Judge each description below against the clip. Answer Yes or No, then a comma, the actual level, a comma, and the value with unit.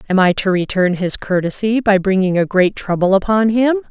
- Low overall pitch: No, high, 200 Hz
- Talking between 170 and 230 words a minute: Yes, average, 200 wpm